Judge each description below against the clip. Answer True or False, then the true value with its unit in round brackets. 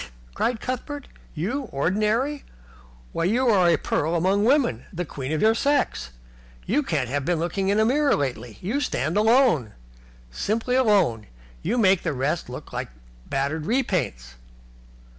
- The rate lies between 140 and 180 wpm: True (150 wpm)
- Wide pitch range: True (8.4 semitones)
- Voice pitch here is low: False (190 Hz)